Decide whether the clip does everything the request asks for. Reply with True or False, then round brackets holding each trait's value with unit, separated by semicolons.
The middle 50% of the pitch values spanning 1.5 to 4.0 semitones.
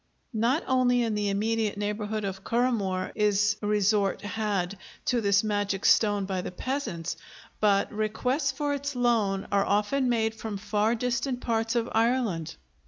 True (3.0 semitones)